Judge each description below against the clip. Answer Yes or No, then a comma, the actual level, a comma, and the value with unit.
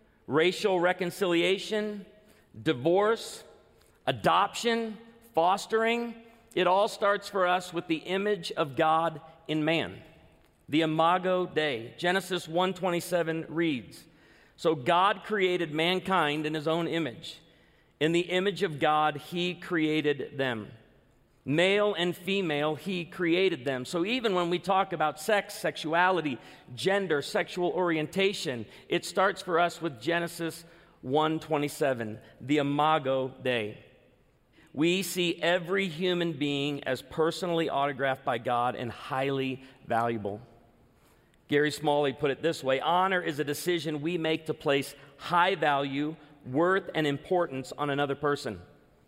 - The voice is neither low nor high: Yes, medium, 165 Hz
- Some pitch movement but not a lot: Yes, average, 3.8 semitones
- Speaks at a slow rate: Yes, slow, 125 wpm